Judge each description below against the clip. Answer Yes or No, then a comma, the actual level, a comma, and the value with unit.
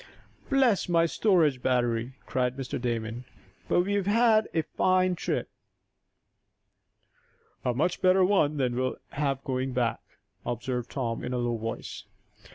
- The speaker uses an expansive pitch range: Yes, wide, 6.9 semitones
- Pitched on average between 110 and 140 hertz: Yes, low, 135 Hz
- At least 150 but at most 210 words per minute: No, average, 140 wpm